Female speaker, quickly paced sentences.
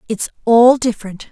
No: female; slow, 135 wpm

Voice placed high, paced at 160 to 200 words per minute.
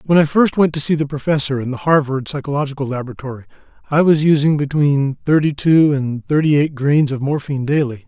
No: medium, 145 Hz; average, 195 wpm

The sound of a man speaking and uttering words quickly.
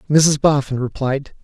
No: male; slow, 125 wpm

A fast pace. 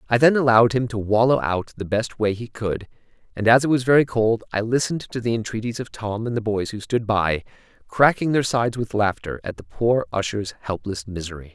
Yes: fast, 220 wpm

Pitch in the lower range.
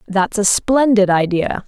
No: high, 205 Hz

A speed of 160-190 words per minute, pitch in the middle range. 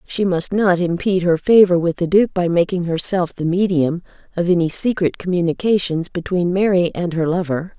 Yes: average, 175 wpm; medium, 175 Hz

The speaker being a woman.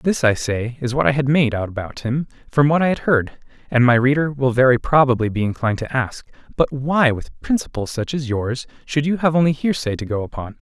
No: male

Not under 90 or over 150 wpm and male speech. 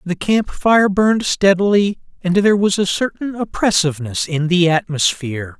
Yes: average, 140 wpm; male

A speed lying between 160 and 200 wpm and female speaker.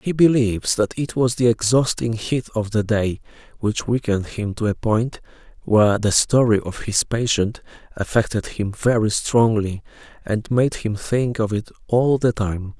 No: average, 170 wpm; male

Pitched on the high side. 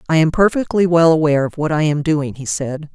No: medium, 155 Hz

